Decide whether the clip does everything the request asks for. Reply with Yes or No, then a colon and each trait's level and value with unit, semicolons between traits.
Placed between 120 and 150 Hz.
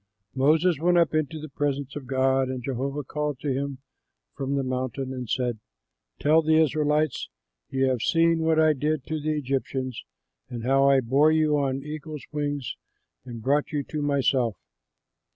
Yes: medium, 140 Hz